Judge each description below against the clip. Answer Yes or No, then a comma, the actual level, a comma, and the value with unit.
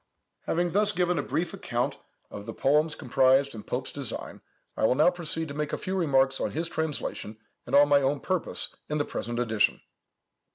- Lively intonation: No, average, 3.8 semitones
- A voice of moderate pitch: Yes, medium, 145 Hz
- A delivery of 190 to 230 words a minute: Yes, average, 195 wpm